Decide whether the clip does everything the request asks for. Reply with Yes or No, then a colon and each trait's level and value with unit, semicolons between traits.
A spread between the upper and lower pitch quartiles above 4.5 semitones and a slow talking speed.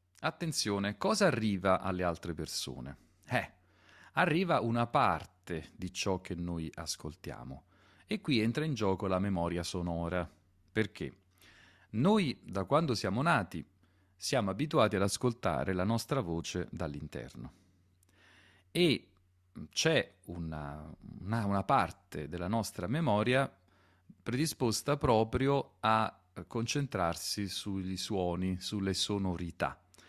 No: average, 3.9 semitones; slow, 110 wpm